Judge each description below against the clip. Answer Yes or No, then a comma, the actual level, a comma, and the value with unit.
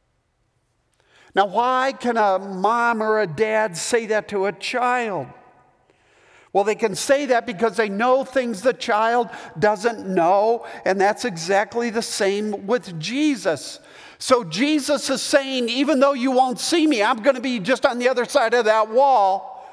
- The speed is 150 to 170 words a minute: Yes, average, 165 wpm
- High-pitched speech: Yes, high, 235 Hz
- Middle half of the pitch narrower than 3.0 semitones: No, average, 4.2 semitones